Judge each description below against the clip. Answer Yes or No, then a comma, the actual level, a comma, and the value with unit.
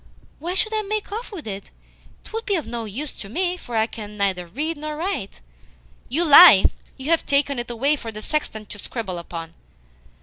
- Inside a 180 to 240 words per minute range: Yes, average, 200 wpm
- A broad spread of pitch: Yes, wide, 8.2 semitones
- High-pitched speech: Yes, very high, 275 Hz